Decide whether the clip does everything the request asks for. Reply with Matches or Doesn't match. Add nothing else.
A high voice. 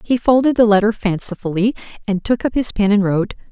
Matches